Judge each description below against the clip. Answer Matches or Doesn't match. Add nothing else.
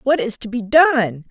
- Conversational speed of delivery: Doesn't match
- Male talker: Doesn't match